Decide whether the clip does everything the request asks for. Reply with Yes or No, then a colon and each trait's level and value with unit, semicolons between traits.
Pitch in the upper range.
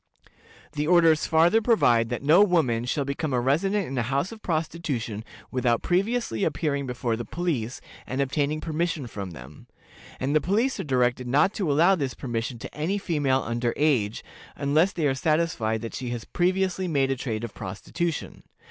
No: medium, 140 Hz